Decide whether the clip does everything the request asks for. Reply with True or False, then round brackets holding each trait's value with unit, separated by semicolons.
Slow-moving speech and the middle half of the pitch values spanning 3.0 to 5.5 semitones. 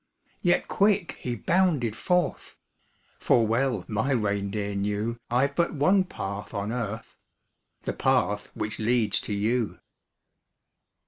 True (120 wpm; 5.1 semitones)